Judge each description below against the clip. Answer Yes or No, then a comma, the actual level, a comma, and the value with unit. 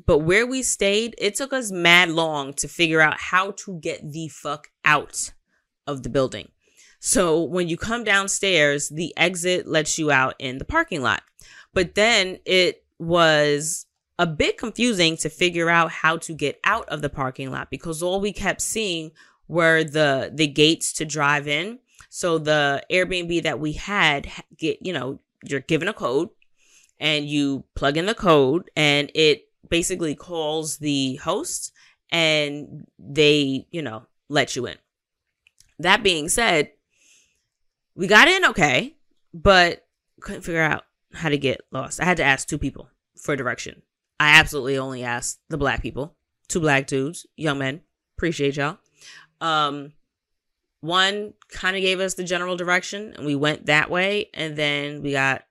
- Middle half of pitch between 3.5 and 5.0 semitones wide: Yes, average, 4.0 semitones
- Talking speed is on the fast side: No, average, 165 wpm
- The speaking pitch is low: No, medium, 160 Hz